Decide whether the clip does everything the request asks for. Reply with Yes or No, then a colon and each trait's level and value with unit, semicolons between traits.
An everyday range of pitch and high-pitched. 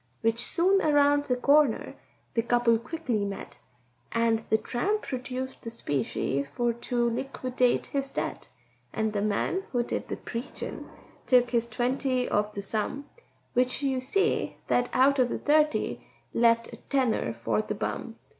Yes: average, 3.1 semitones; high, 245 Hz